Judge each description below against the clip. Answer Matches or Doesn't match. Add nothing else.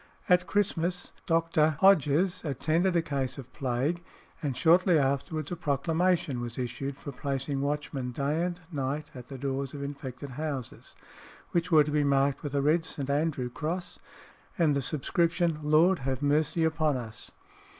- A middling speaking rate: Matches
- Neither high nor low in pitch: Matches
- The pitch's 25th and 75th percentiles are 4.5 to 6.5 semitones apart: Doesn't match